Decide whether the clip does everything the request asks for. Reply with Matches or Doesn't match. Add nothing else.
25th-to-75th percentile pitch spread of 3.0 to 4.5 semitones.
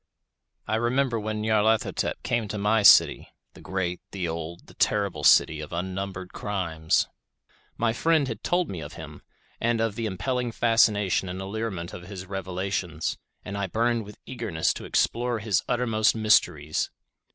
Matches